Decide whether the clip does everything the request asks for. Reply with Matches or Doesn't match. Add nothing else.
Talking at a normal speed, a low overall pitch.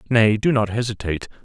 Matches